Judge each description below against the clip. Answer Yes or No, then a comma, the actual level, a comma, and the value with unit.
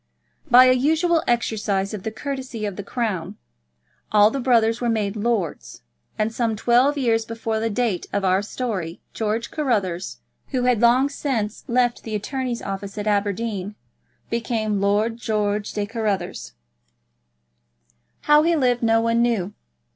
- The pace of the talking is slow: No, average, 150 wpm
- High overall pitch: Yes, high, 225 Hz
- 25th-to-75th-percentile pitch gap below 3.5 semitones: Yes, average, 3.0 semitones